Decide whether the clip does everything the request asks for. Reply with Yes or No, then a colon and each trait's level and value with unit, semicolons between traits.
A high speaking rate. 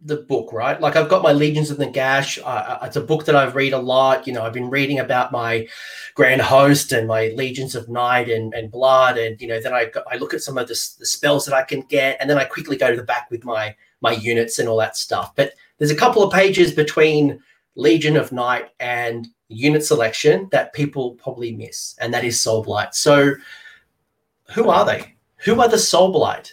Yes: fast, 230 wpm